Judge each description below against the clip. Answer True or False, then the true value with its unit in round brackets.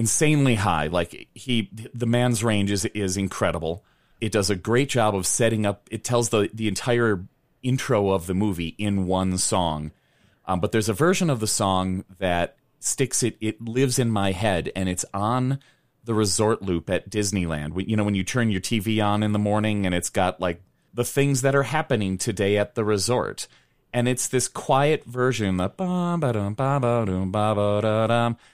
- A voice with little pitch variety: False (3.9 semitones)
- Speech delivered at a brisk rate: False (175 wpm)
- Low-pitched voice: True (110 Hz)